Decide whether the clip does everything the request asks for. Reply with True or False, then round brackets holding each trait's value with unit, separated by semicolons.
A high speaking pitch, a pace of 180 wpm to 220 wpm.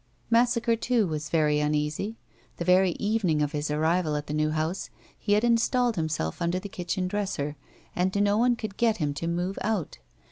False (180 Hz; 185 wpm)